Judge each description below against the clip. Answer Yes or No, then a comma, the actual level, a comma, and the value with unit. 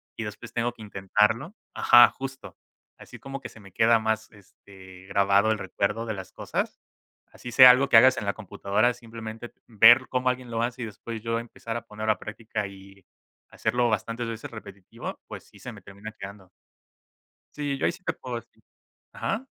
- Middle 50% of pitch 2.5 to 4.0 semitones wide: Yes, average, 3.1 semitones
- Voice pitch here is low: Yes, low, 115 Hz